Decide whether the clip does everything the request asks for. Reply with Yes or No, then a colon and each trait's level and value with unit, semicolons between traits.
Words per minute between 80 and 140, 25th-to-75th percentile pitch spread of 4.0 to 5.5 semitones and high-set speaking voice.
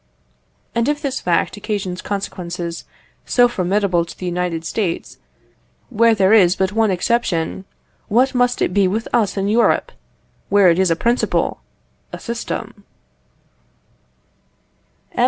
Yes: slow, 135 wpm; average, 4.3 semitones; high, 200 Hz